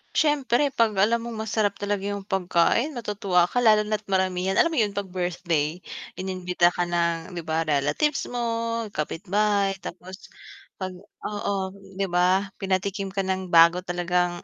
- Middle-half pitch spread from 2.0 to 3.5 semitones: Yes, average, 3.0 semitones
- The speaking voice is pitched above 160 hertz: Yes, high, 190 Hz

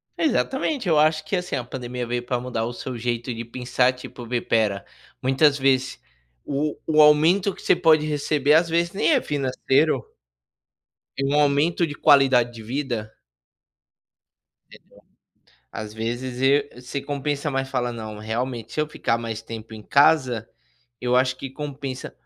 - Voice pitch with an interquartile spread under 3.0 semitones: No, average, 3.7 semitones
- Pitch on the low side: Yes, low, 130 Hz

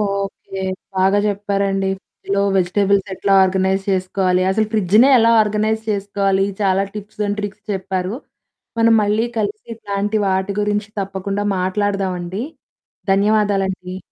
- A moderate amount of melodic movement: No, narrow, 1.4 semitones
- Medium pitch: No, high, 200 Hz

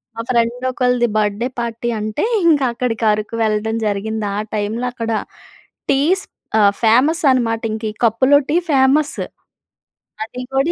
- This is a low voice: No, high, 235 Hz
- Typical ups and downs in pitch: Yes, average, 3.1 semitones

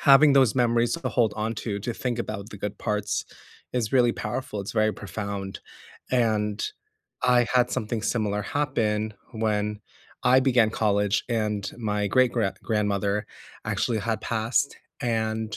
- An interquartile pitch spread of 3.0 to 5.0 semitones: No, narrow, 2.5 semitones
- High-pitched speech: No, low, 110 Hz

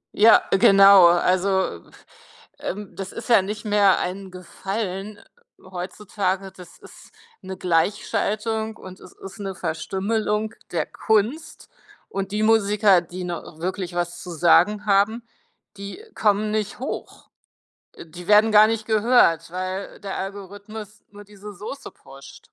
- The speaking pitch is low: No, high, 200 Hz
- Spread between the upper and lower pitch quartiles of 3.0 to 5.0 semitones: No, narrow, 2.4 semitones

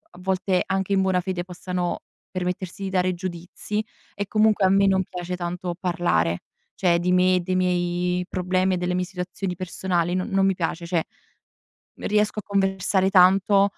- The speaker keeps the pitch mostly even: Yes, narrow, 1.3 semitones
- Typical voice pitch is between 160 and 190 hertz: Yes, medium, 185 Hz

